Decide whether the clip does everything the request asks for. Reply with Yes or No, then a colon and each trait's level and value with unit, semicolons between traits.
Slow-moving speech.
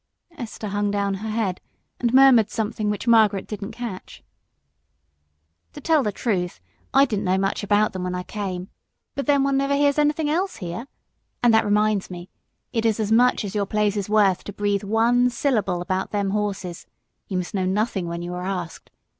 No: average, 190 wpm